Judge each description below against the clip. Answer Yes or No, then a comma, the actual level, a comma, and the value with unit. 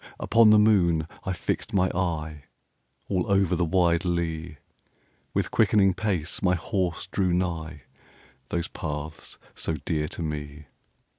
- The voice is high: No, very low, 85 Hz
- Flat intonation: No, average, 3.1 semitones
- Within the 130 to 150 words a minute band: Yes, average, 140 wpm